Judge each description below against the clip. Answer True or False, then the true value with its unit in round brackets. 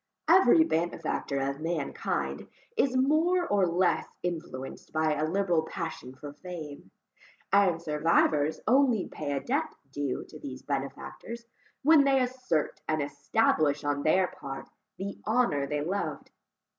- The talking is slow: True (130 wpm)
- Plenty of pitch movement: True (7.9 semitones)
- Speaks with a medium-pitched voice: True (165 Hz)